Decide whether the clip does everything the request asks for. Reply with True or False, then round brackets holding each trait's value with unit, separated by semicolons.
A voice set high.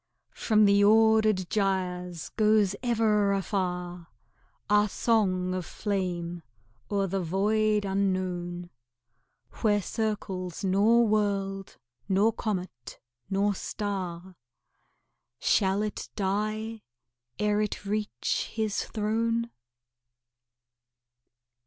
True (200 Hz)